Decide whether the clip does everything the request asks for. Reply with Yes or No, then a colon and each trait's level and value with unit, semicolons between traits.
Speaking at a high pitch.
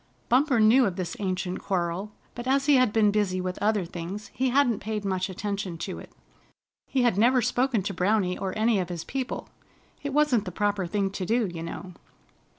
Yes: high, 205 Hz